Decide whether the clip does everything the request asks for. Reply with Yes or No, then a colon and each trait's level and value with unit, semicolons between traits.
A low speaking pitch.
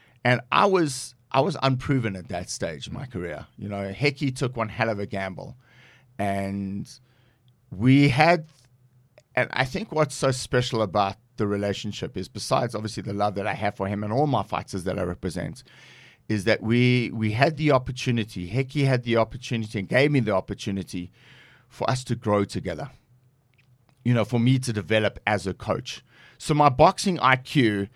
Yes: low, 120 Hz